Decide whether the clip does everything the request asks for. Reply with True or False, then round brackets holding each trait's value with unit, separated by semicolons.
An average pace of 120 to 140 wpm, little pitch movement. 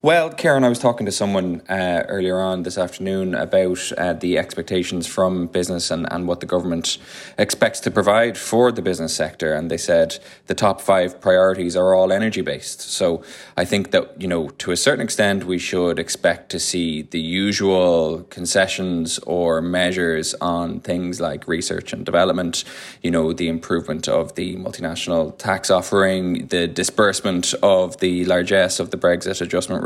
False (170 wpm; 1.7 semitones)